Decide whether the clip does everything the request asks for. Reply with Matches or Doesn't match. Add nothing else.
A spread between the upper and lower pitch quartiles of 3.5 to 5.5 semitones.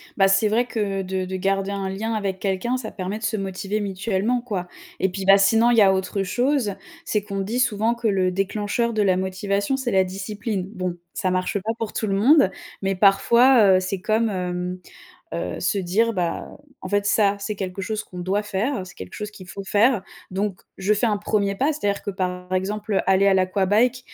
Doesn't match